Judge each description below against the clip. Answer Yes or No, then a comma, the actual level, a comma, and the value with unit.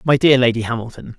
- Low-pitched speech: Yes, low, 125 Hz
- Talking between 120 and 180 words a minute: No, fast, 205 wpm